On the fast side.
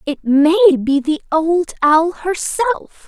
No: slow, 135 wpm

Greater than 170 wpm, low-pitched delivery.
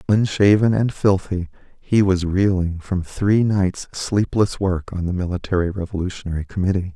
No: average, 140 wpm; very low, 95 Hz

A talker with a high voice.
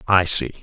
No: very low, 90 Hz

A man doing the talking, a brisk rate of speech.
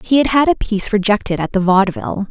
No: female; fast, 235 wpm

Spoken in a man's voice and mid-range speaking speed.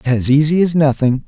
Yes: male; average, 190 wpm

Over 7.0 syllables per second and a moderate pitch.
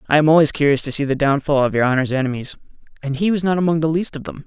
Yes: 7.2 syllables/s; medium, 150 Hz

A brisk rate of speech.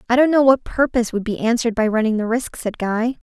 Yes: fast, 255 wpm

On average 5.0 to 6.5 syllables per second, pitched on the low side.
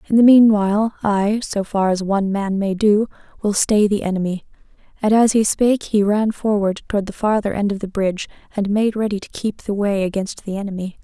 No: 5.5 syllables/s; high, 205 Hz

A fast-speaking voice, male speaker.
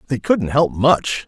No: average, 190 wpm; male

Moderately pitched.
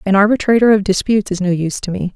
No: high, 200 Hz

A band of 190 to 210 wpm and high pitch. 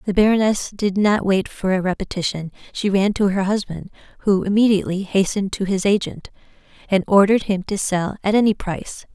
No: average, 175 wpm; high, 195 Hz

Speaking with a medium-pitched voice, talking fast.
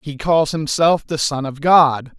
No: medium, 150 Hz; average, 190 wpm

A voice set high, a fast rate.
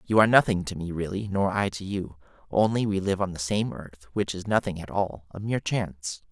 No: very low, 95 Hz; fast, 230 wpm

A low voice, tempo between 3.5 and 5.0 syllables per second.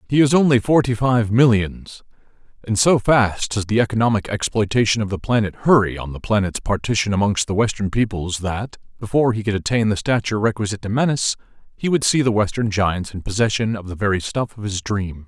No: low, 110 Hz; 5.9 syllables/s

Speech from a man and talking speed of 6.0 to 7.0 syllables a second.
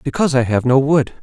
Yes: male; 6.5 syllables/s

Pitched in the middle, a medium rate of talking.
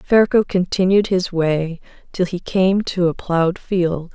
Yes: medium, 180 Hz; average, 160 wpm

